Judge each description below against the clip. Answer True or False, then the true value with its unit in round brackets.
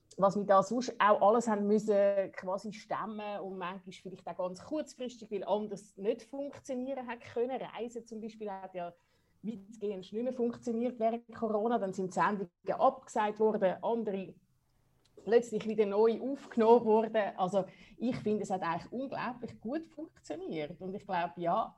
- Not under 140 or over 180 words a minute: True (160 wpm)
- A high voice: True (215 Hz)